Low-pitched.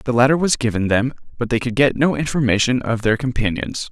Yes: low, 125 Hz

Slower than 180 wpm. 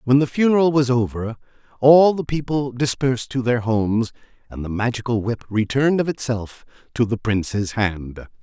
Yes: average, 165 wpm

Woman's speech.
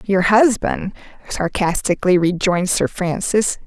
Yes: female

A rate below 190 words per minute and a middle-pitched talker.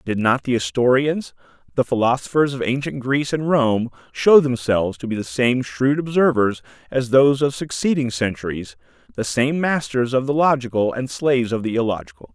No: average, 170 wpm; low, 125 Hz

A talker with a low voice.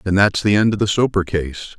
Yes: low, 100 Hz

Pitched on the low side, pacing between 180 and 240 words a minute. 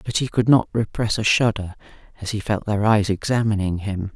Yes: low, 105 Hz; average, 200 wpm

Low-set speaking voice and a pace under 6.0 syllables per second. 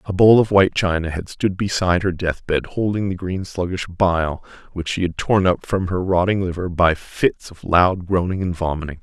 Yes: very low, 90 Hz; 4.9 syllables/s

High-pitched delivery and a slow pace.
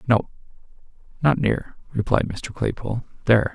No: low, 120 Hz; slow, 120 wpm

